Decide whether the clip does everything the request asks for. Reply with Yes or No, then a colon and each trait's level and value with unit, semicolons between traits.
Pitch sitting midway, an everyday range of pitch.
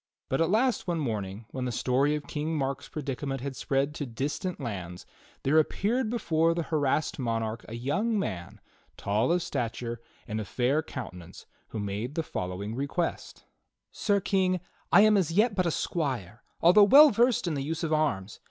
No: medium, 145 Hz; wide, 6.8 semitones